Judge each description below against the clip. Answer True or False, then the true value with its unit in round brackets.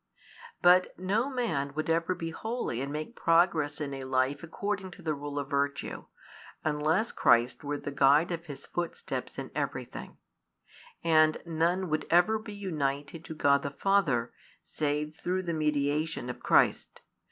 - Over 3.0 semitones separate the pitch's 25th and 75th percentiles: True (3.8 semitones)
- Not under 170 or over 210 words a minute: False (155 wpm)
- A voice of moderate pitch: True (155 Hz)